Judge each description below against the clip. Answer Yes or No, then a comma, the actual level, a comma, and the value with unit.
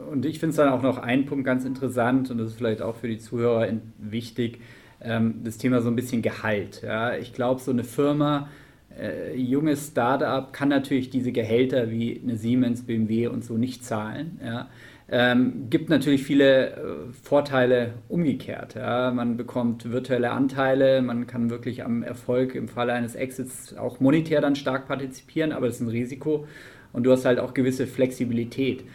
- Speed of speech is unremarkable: Yes, average, 165 wpm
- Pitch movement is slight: Yes, narrow, 2.1 semitones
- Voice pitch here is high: No, low, 125 Hz